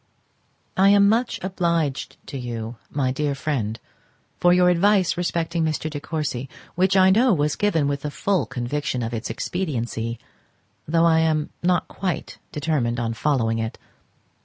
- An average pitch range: No, wide, 6.0 semitones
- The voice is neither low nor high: Yes, medium, 155 Hz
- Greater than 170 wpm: No, average, 155 wpm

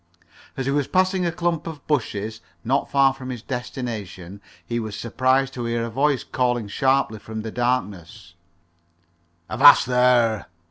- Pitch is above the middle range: No, low, 125 Hz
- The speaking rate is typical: Yes, average, 150 wpm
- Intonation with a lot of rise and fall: No, average, 3.6 semitones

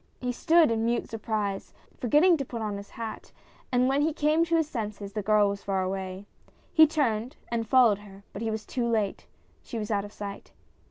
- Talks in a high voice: Yes, high, 225 Hz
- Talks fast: Yes, fast, 215 wpm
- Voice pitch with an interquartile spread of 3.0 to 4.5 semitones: Yes, average, 4.0 semitones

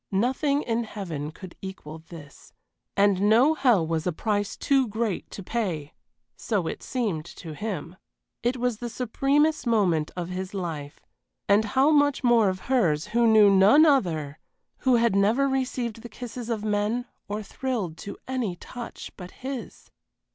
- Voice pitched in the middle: No, high, 215 Hz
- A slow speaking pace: No, average, 160 wpm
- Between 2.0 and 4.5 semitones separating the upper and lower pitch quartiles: No, average, 5.3 semitones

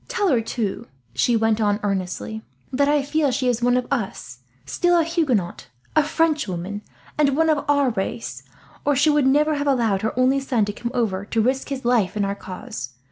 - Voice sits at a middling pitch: No, high, 245 Hz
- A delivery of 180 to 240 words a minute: Yes, average, 200 wpm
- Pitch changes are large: Yes, wide, 5.9 semitones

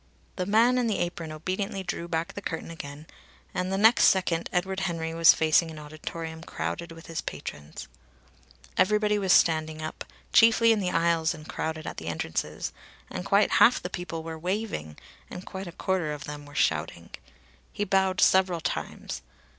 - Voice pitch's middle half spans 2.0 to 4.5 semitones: Yes, average, 3.3 semitones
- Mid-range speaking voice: Yes, medium, 170 Hz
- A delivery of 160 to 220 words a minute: Yes, average, 175 wpm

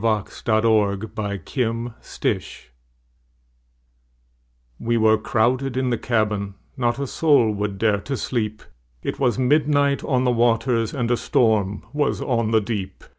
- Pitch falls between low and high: No, low, 115 Hz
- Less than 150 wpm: No, average, 155 wpm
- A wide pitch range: No, average, 2.9 semitones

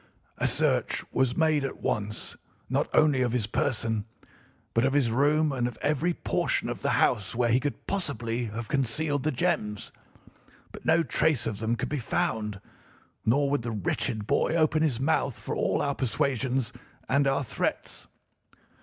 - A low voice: Yes, low, 130 Hz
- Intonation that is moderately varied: Yes, average, 4.2 semitones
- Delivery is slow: No, average, 170 wpm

